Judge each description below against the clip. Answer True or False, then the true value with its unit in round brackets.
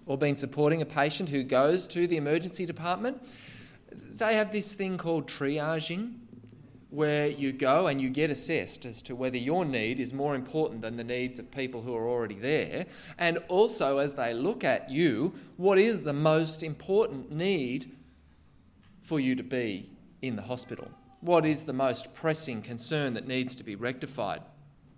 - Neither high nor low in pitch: True (145 Hz)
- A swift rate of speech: False (175 wpm)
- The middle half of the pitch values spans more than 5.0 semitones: False (4.5 semitones)